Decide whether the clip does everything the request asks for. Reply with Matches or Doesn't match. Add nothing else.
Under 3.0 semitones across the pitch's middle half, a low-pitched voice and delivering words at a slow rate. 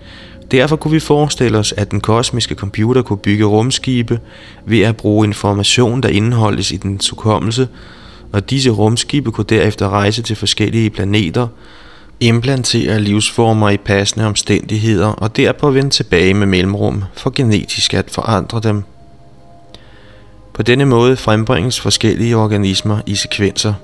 Matches